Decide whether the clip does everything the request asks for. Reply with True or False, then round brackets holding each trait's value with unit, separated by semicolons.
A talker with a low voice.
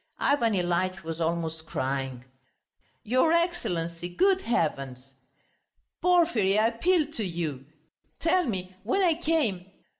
False (190 Hz)